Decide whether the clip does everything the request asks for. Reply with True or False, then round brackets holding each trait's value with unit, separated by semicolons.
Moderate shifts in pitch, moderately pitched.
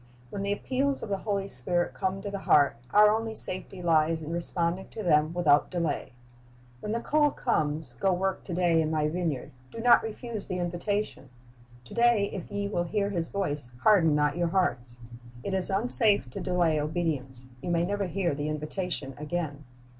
True (4.6 semitones; 175 Hz)